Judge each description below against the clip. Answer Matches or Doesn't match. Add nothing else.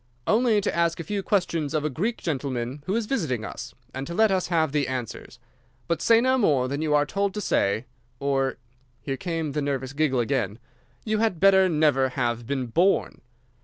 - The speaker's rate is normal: Matches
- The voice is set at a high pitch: Doesn't match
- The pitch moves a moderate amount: Doesn't match